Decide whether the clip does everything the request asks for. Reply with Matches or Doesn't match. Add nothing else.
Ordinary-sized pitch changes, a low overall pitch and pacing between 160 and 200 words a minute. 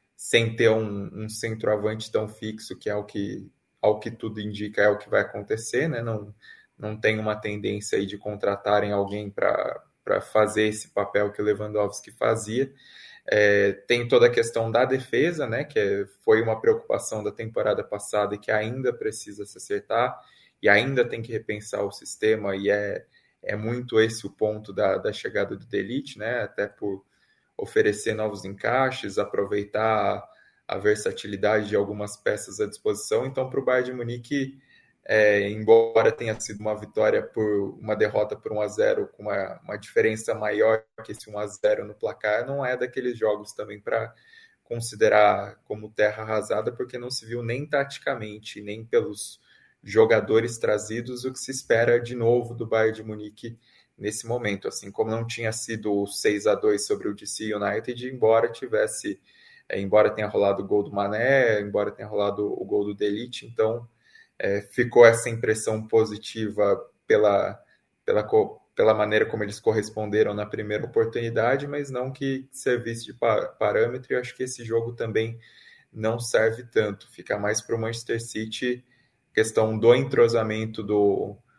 Matches